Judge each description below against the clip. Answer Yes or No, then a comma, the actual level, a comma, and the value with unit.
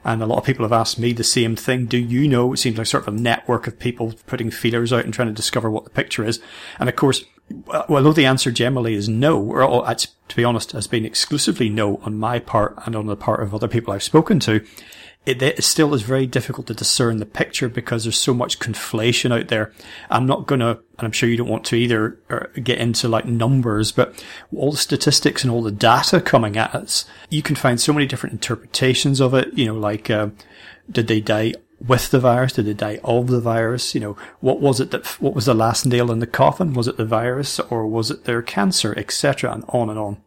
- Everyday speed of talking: No, fast, 240 wpm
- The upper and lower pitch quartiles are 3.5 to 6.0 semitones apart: No, average, 2.8 semitones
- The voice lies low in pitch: Yes, low, 120 Hz